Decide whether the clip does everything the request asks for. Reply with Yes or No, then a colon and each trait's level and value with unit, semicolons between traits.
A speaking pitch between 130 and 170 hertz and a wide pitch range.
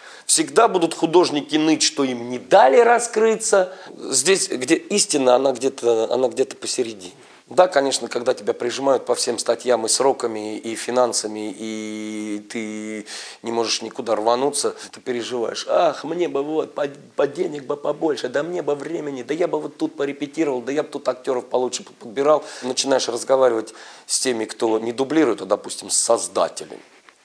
Yes: low, 135 Hz; wide, 5.8 semitones